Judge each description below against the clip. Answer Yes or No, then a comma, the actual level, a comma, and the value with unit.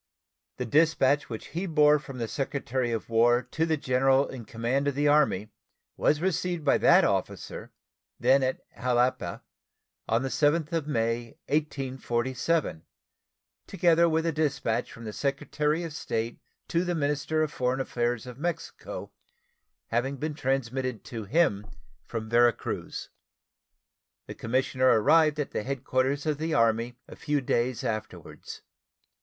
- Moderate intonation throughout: Yes, average, 4.1 semitones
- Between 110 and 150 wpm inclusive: Yes, average, 145 wpm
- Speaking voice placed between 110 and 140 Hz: Yes, low, 135 Hz